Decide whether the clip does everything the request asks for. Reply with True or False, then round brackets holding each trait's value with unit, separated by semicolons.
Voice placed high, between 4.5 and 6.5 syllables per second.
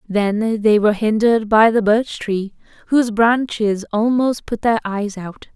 False (220 Hz; 4.3 syllables/s)